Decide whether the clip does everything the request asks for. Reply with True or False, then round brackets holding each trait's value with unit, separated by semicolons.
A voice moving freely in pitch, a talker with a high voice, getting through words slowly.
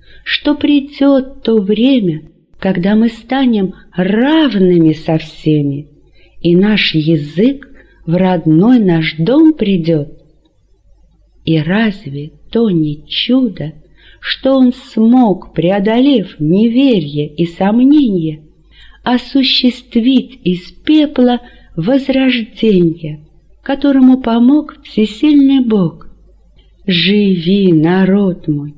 True (7.5 semitones; 195 Hz; 85 wpm)